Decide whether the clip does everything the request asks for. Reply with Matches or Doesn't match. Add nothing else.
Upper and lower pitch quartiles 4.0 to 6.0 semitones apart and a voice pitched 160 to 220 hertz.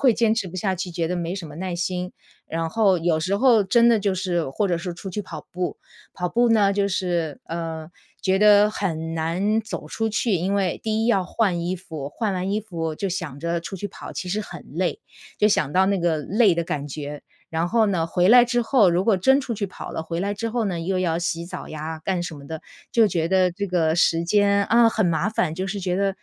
Doesn't match